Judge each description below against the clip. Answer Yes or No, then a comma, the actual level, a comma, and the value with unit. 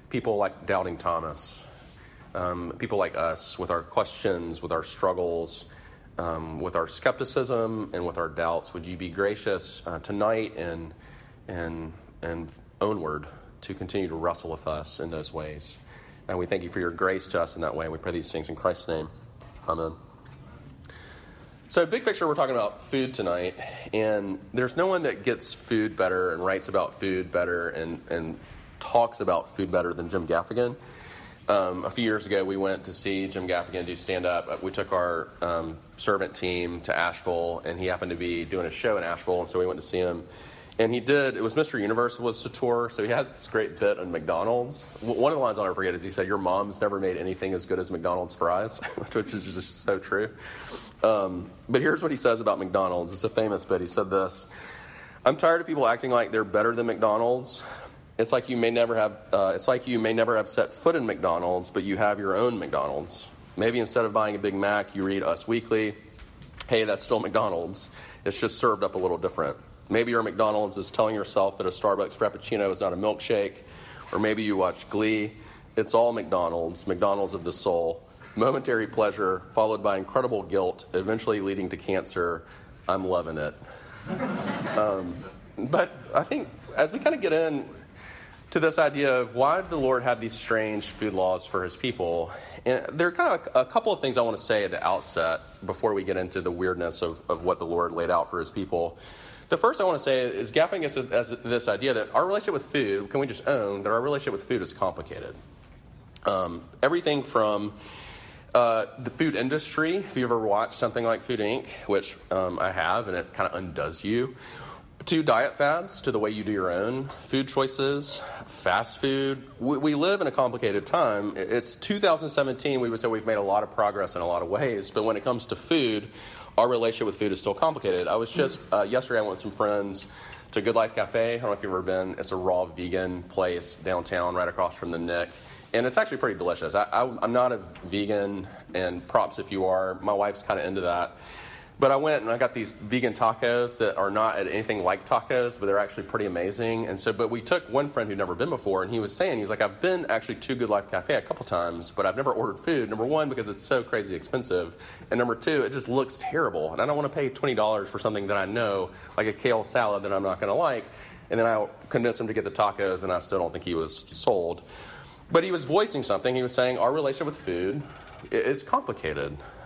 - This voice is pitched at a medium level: No, low, 105 Hz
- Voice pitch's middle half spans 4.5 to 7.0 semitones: Yes, average, 5.2 semitones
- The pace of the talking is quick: Yes, fast, 215 wpm